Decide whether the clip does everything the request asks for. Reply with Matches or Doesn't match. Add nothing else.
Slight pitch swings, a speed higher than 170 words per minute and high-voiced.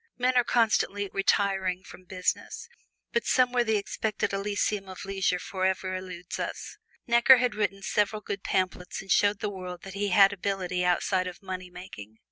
Doesn't match